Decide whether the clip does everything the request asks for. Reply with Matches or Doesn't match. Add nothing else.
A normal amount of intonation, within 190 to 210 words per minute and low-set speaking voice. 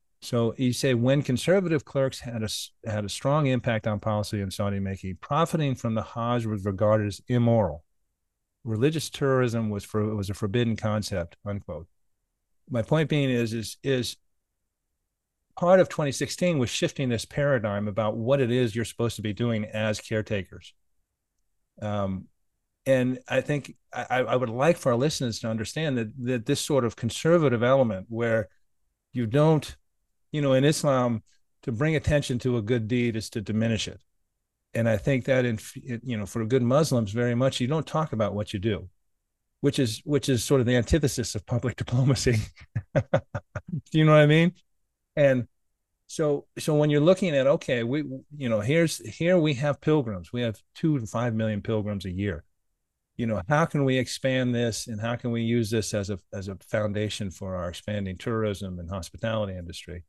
Doesn't match